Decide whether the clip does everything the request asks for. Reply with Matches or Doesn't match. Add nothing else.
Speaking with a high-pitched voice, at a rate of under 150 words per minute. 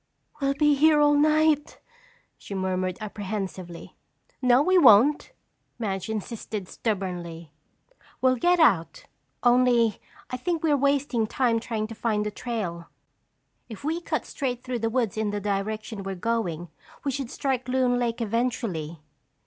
Matches